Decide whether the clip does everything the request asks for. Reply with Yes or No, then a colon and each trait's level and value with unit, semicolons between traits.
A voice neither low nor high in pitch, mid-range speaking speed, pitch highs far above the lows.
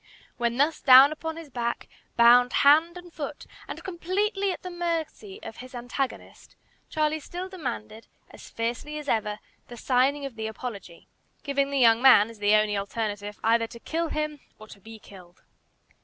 No: very high, 255 Hz; average, 170 wpm; wide, 5.7 semitones